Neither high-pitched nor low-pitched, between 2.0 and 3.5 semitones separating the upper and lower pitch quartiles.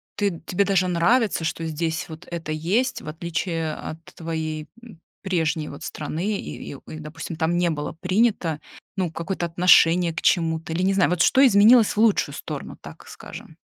Yes: medium, 170 Hz; average, 3.2 semitones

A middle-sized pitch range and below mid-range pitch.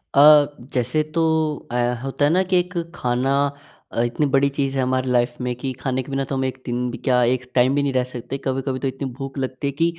No: narrow, 1.7 semitones; low, 130 Hz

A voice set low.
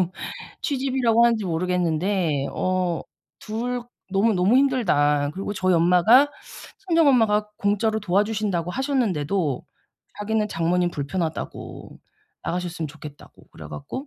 No: high, 195 Hz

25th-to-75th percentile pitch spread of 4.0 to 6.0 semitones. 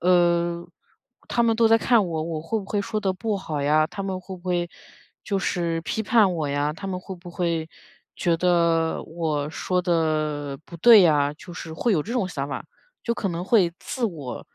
No: average, 3.6 semitones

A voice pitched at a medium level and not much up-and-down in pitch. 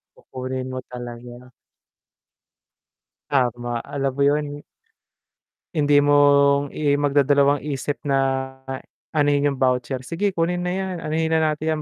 Yes: medium, 145 Hz; narrow, 2.3 semitones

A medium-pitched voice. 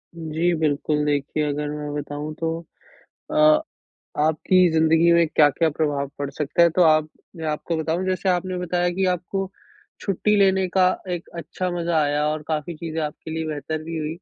Yes: medium, 160 Hz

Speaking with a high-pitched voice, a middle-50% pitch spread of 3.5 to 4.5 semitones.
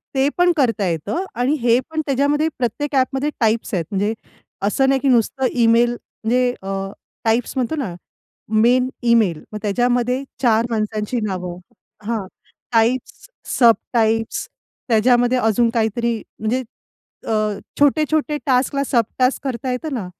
No: high, 240 Hz; average, 3.1 semitones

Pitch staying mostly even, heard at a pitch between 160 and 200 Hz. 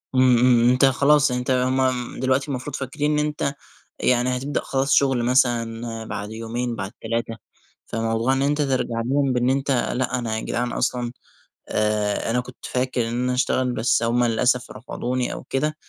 No: narrow, 2.0 semitones; low, 125 Hz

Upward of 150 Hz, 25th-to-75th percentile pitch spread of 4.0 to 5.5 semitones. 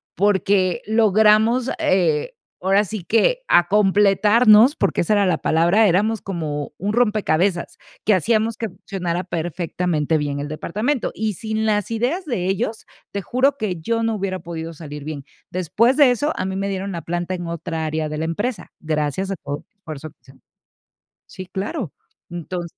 Yes: high, 190 Hz; average, 4.5 semitones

